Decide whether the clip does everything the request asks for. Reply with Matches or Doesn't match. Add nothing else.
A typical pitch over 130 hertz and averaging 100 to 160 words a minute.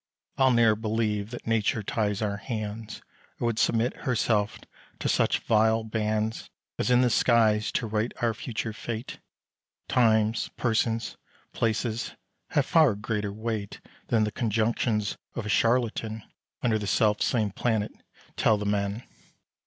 Doesn't match